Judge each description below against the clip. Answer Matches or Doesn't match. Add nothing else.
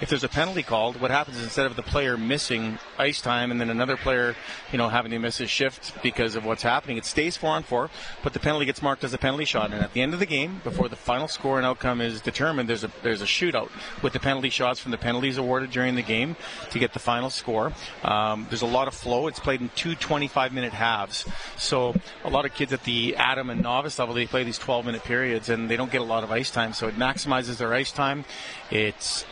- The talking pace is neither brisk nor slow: Doesn't match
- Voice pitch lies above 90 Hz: Matches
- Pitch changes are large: Doesn't match